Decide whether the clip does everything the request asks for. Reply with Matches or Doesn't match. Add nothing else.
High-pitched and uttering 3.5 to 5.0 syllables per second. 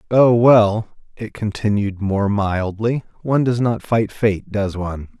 Doesn't match